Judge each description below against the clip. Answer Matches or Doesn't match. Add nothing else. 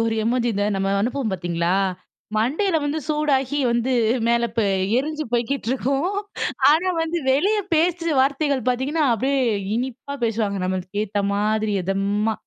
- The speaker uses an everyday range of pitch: Doesn't match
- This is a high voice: Matches